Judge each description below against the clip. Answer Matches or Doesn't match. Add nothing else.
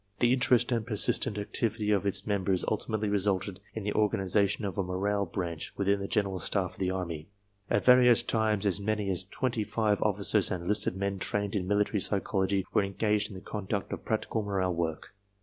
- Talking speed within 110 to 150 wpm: Doesn't match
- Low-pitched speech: Matches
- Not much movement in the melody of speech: Matches